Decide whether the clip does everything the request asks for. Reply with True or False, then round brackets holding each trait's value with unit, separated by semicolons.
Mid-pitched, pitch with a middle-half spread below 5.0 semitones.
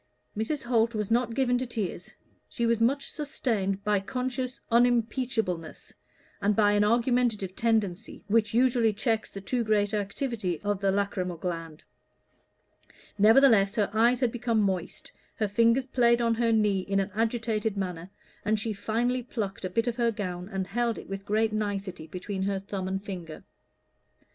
False (215 Hz; 3.2 semitones)